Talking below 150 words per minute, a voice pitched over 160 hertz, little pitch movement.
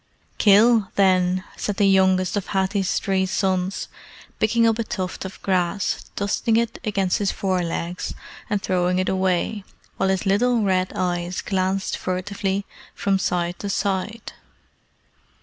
Yes: average, 140 wpm; high, 190 Hz; narrow, 1.8 semitones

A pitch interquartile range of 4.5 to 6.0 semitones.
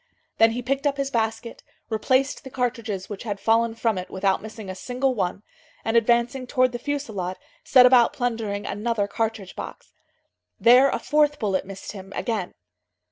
No: average, 3.8 semitones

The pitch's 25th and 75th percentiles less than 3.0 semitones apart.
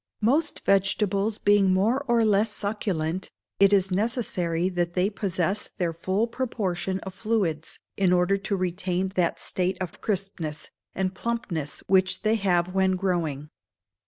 Yes: narrow, 2.5 semitones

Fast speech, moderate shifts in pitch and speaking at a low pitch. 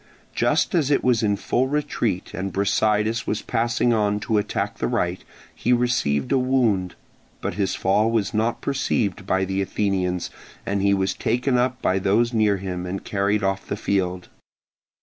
No: average, 170 wpm; average, 3.5 semitones; low, 105 Hz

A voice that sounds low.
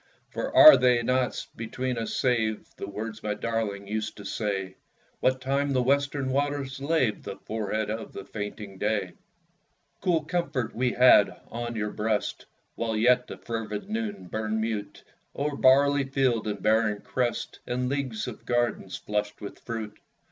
Yes: low, 115 Hz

